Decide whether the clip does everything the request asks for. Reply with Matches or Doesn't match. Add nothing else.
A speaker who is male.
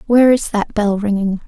Doesn't match